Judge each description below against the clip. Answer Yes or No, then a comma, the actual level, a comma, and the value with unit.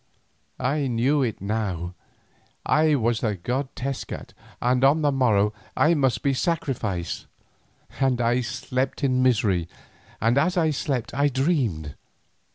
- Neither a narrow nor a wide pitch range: Yes, average, 4.0 semitones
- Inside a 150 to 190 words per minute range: No, slow, 135 wpm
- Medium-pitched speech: No, low, 130 Hz